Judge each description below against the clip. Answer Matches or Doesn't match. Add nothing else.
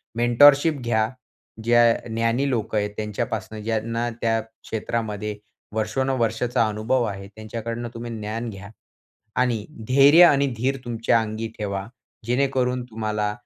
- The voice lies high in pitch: Doesn't match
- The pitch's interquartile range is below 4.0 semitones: Matches